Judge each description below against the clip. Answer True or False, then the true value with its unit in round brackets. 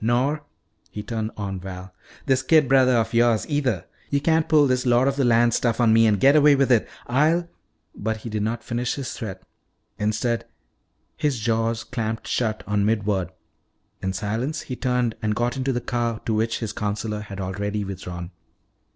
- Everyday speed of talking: True (190 wpm)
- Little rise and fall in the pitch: False (3.4 semitones)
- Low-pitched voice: True (115 Hz)